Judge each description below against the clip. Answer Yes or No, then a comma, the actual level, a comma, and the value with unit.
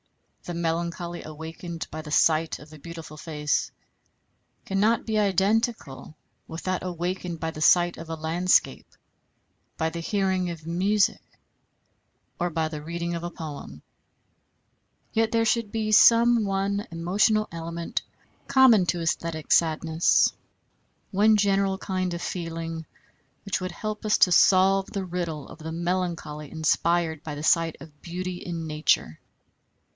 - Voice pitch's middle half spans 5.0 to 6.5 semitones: No, average, 3.2 semitones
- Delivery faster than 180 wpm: No, average, 140 wpm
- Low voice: No, medium, 170 Hz